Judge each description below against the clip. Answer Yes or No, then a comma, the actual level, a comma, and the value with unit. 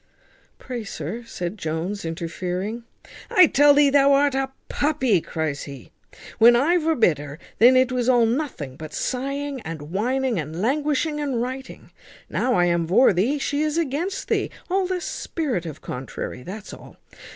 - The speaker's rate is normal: Yes, average, 160 wpm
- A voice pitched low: No, high, 240 Hz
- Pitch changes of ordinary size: No, wide, 8.5 semitones